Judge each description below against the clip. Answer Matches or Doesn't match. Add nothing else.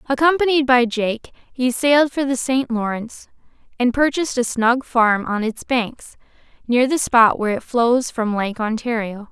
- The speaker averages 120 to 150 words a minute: Doesn't match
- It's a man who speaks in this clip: Doesn't match